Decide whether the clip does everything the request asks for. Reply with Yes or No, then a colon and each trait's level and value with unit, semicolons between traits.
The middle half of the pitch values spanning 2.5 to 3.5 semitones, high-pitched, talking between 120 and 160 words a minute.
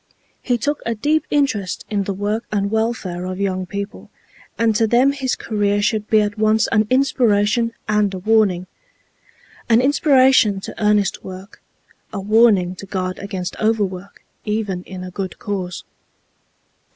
Yes: average, 2.9 semitones; high, 210 Hz; average, 150 wpm